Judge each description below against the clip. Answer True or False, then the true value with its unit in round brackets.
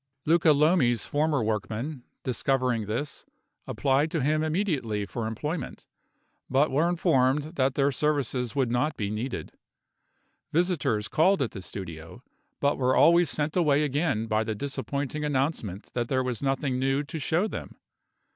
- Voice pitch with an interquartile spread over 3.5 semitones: True (4.2 semitones)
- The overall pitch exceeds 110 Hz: True (140 Hz)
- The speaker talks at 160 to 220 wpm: False (145 wpm)